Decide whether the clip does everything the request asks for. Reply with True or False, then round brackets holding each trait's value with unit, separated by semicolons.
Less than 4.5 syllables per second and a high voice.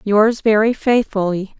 True (4.1 syllables/s; 215 Hz)